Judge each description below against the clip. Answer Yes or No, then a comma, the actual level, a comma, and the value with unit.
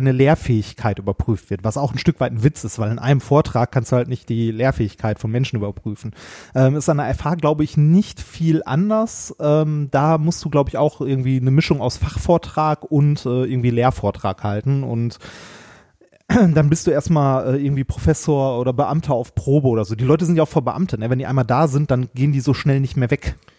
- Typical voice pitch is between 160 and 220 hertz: No, low, 135 Hz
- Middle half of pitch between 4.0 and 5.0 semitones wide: Yes, average, 4.3 semitones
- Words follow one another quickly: Yes, fast, 220 wpm